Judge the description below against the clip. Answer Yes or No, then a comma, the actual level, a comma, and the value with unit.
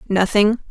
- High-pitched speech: Yes, high, 205 Hz